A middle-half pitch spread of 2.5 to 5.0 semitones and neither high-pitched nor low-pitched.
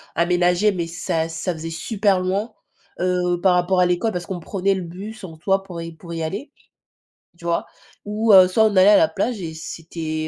Yes: average, 2.9 semitones; medium, 180 Hz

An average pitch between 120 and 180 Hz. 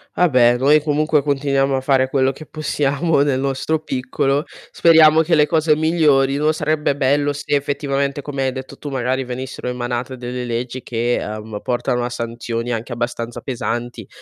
Yes: low, 135 Hz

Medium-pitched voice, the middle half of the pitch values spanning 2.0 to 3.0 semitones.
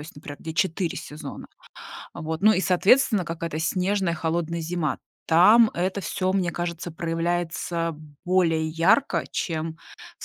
Yes: medium, 170 Hz; narrow, 2.4 semitones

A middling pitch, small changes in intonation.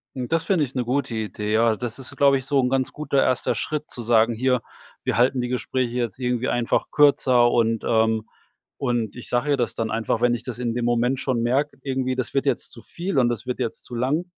No: low, 125 Hz; narrow, 2.3 semitones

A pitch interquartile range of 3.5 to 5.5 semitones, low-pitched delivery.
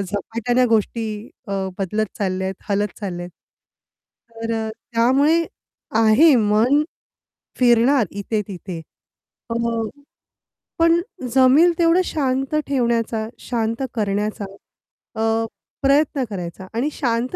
No: average, 4.2 semitones; high, 230 Hz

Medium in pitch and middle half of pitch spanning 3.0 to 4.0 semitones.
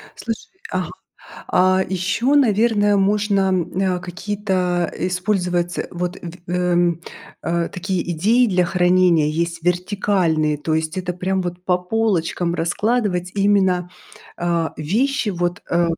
No: medium, 180 Hz; narrow, 2.5 semitones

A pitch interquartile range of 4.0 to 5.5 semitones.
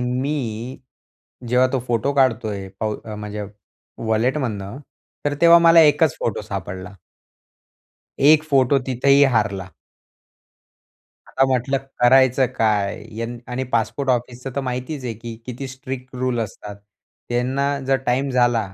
No: average, 3.2 semitones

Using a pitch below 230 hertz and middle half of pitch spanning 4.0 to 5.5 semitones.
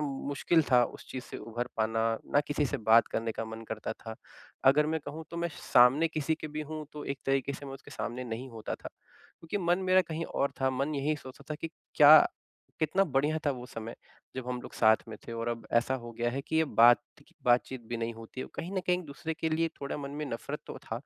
Yes: low, 135 Hz; average, 4.6 semitones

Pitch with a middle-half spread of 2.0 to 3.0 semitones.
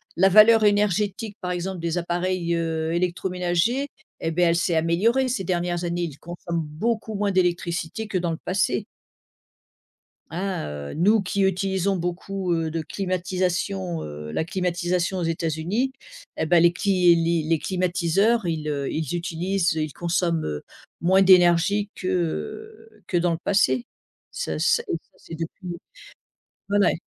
Yes: narrow, 2.6 semitones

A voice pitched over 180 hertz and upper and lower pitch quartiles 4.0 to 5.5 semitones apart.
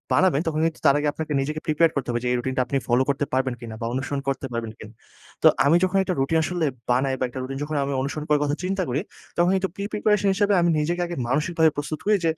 No: medium, 150 Hz; average, 4.6 semitones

